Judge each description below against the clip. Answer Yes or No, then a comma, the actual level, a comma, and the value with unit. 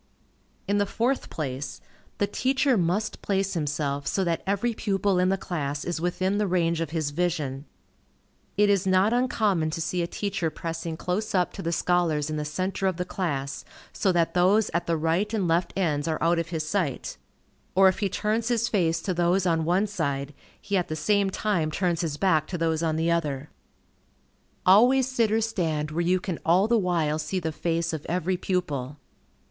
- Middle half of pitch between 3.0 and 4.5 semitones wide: Yes, average, 3.6 semitones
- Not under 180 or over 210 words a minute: Yes, average, 195 wpm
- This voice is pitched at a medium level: Yes, medium, 175 Hz